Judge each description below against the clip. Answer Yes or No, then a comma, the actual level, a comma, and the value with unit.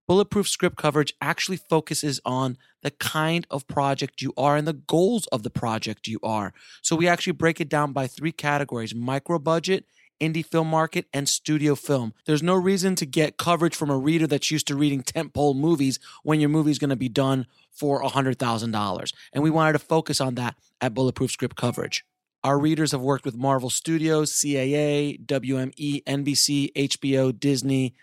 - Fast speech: No, average, 185 wpm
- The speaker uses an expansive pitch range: No, average, 3.1 semitones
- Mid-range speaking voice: Yes, medium, 145 Hz